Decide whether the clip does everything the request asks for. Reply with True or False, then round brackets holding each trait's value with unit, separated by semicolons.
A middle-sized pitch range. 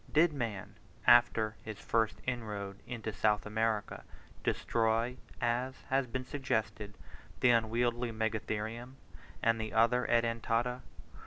False (2.0 semitones)